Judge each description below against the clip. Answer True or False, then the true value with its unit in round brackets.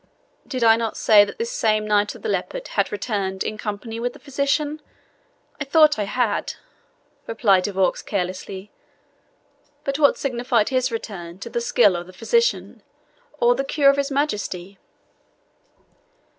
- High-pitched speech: True (230 Hz)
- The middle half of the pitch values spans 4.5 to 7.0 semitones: True (5.4 semitones)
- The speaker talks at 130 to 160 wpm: True (155 wpm)